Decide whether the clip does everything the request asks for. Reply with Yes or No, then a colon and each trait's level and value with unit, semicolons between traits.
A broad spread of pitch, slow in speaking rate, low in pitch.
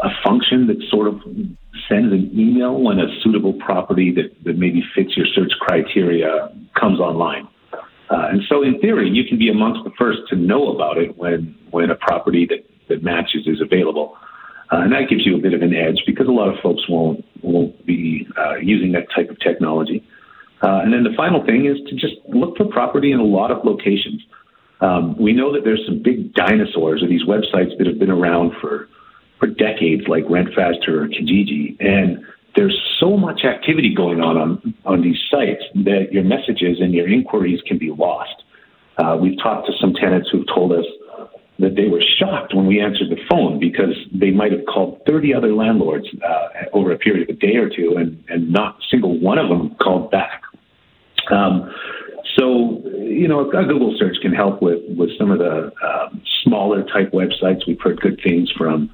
No: wide, 8.5 semitones; average, 200 wpm; low, 100 Hz